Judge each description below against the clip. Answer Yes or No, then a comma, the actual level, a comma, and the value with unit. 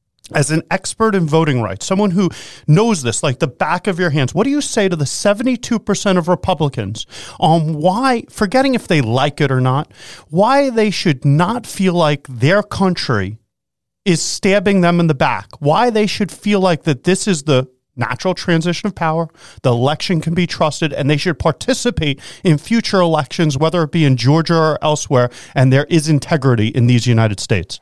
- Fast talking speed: No, average, 190 wpm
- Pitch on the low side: No, medium, 160 Hz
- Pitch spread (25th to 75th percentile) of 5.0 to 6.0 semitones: Yes, wide, 5.4 semitones